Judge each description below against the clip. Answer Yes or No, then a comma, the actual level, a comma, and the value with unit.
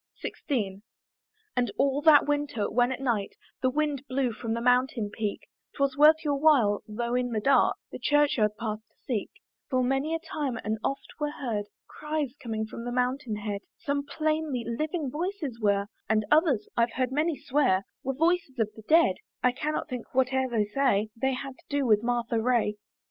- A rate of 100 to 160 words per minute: No, average, 185 wpm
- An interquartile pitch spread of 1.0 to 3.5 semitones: No, average, 4.4 semitones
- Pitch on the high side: Yes, very high, 255 Hz